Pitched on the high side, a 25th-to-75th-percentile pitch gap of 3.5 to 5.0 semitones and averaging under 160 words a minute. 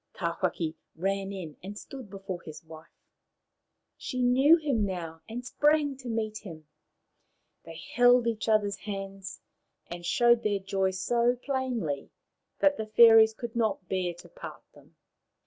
Yes: high, 210 Hz; average, 4.5 semitones; average, 145 wpm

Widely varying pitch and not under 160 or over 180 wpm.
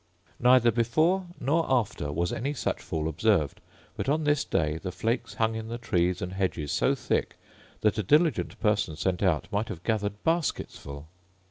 Yes: wide, 6.4 semitones; average, 175 wpm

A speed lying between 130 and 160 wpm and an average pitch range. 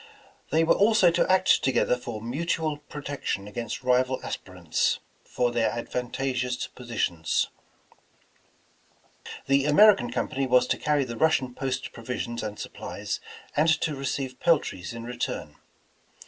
Yes: slow, 135 wpm; average, 3.8 semitones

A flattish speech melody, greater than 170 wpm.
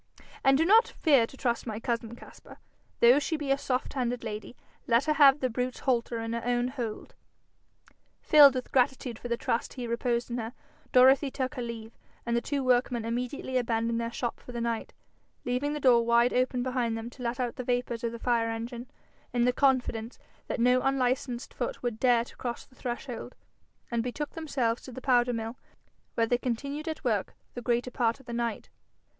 Yes: narrow, 1.8 semitones; average, 200 wpm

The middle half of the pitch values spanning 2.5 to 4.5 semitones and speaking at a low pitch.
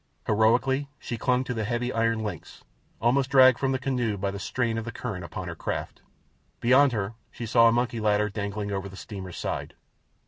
Yes: average, 3.5 semitones; low, 115 Hz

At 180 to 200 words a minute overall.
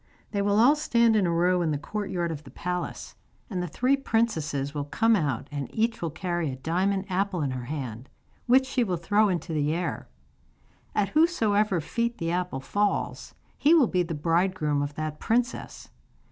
Yes: average, 190 wpm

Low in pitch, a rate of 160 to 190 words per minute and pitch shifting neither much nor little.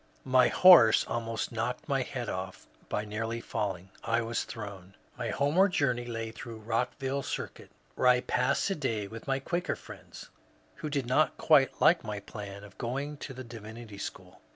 Yes: low, 120 Hz; average, 175 wpm; average, 3.7 semitones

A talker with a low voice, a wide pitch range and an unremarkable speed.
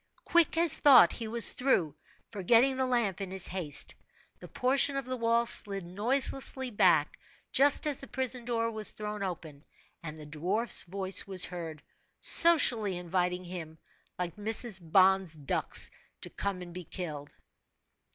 No: high, 200 Hz; wide, 5.7 semitones; average, 150 wpm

